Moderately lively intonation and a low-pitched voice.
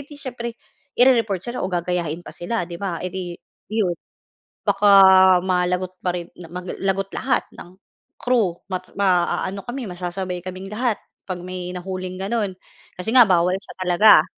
No: average, 3.1 semitones; medium, 185 Hz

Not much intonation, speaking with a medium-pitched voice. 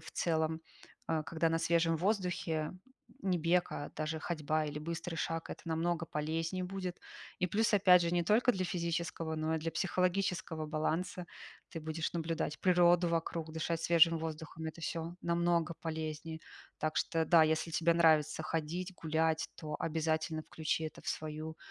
Yes: narrow, 1.5 semitones; medium, 165 Hz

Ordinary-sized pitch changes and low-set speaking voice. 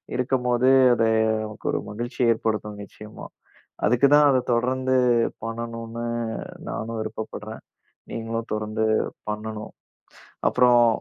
No: narrow, 2.2 semitones; low, 115 Hz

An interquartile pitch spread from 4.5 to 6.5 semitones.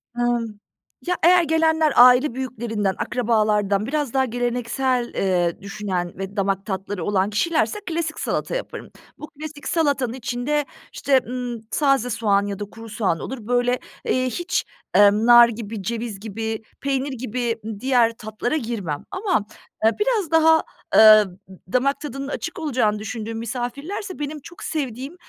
Yes: average, 5.0 semitones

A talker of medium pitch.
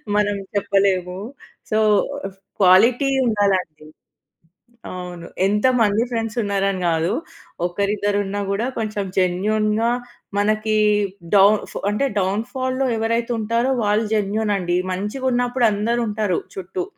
No: high, 205 Hz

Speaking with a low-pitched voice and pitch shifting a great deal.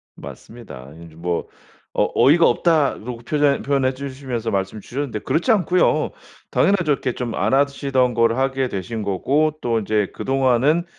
No: low, 130 Hz; average, 4.0 semitones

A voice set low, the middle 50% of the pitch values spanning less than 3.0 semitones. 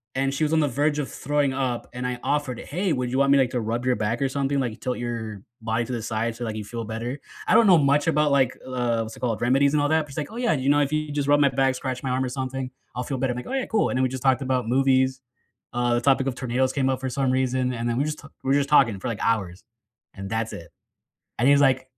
Yes: low, 130 Hz; narrow, 2.6 semitones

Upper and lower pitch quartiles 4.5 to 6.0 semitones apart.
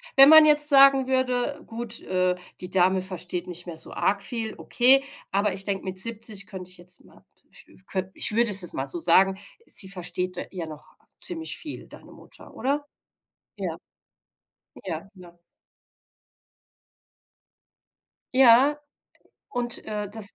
Yes: wide, 5.4 semitones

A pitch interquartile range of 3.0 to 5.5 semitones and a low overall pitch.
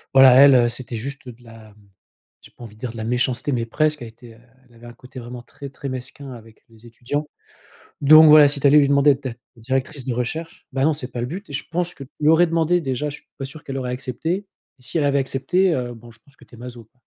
Yes: average, 3.4 semitones; low, 130 Hz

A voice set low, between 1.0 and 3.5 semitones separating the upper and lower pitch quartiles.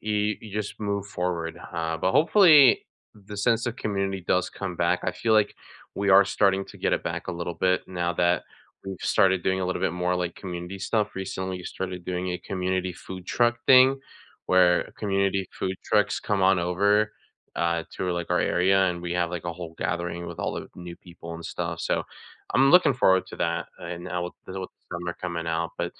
Yes: very low, 95 Hz; narrow, 2.4 semitones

